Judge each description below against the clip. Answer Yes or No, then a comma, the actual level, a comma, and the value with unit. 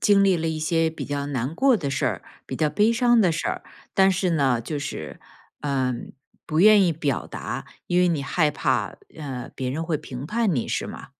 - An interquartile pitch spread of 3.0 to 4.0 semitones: No, average, 4.9 semitones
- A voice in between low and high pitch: Yes, medium, 160 Hz